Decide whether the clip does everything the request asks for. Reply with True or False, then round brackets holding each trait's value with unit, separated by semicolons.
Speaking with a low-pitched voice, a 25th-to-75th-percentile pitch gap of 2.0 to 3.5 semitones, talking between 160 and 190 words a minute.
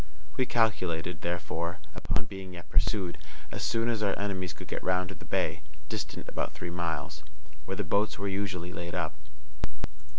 True (90 Hz; 2.7 semitones; 170 wpm)